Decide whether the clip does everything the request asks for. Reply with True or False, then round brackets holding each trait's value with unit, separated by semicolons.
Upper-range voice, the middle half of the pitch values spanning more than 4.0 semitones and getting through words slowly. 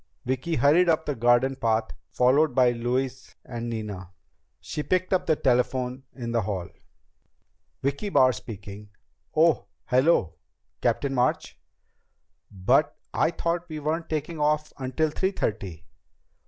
False (130 Hz; 4.9 semitones; 130 wpm)